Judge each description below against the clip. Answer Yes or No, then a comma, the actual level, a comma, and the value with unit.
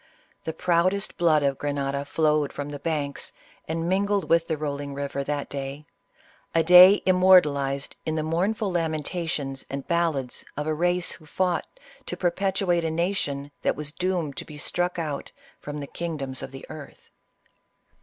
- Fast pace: No, average, 165 wpm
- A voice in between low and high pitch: Yes, medium, 155 Hz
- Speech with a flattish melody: No, average, 3.8 semitones